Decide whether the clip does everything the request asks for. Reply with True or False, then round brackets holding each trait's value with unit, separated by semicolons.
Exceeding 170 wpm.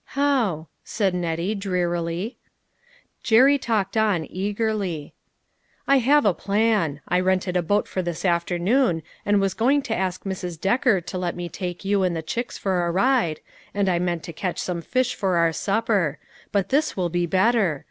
True (180 wpm)